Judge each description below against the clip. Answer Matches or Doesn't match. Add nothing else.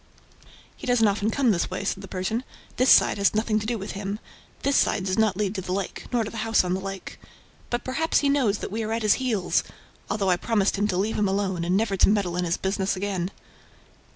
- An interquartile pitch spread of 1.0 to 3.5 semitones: Matches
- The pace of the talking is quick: Matches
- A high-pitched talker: Matches